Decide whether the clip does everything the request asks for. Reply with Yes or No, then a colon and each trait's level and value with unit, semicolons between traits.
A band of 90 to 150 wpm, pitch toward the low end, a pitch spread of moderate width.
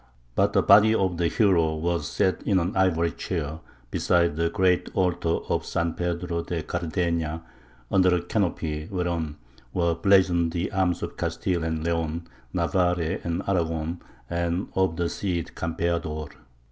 No: average, 145 wpm; very low, 85 Hz; narrow, 1.6 semitones